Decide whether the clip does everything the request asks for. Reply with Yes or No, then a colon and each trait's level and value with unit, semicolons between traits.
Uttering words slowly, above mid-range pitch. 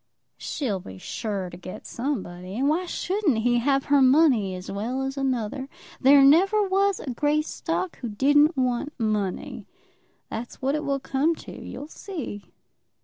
No: average, 155 wpm; very high, 270 Hz